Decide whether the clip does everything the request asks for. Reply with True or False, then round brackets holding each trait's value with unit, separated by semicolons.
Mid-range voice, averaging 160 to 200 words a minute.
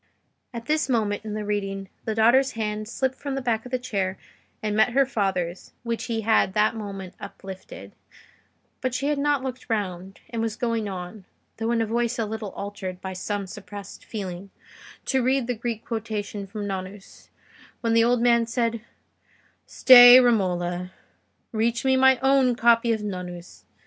False (220 Hz; 170 wpm)